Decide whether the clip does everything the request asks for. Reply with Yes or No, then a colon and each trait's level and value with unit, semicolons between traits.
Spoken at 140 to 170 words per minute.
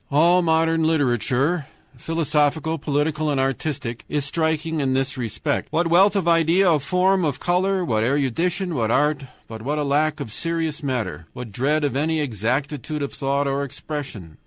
Yes: average, 165 wpm